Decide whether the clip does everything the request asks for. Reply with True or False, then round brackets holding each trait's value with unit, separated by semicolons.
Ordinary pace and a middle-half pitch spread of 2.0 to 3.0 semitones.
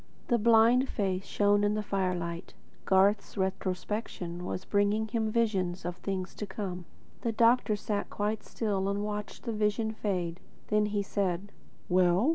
True (150 wpm; 2.5 semitones)